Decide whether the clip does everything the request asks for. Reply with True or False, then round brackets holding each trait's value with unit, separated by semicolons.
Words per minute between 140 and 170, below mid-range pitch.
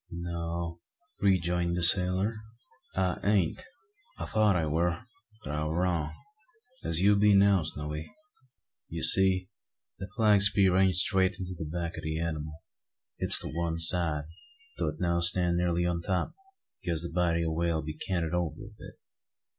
True (165 wpm; 85 Hz)